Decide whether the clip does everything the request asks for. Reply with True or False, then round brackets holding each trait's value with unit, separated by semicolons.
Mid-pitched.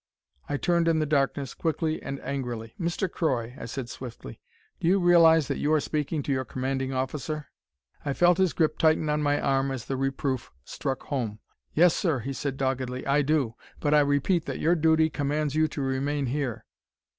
True (145 Hz)